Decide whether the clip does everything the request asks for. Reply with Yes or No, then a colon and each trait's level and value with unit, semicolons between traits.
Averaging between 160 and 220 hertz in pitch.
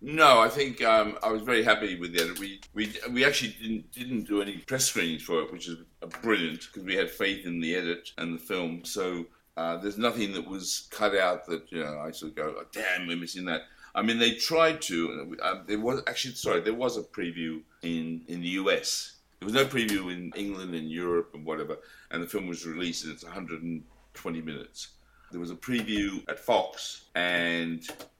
No: very low, 90 Hz